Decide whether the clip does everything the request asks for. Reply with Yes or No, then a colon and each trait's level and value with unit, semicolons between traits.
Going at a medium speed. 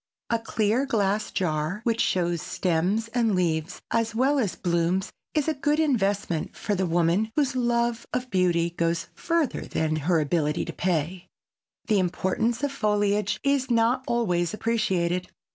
Yes: average, 150 wpm